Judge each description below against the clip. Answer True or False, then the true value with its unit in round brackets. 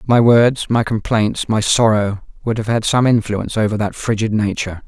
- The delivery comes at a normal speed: True (185 wpm)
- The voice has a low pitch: True (110 Hz)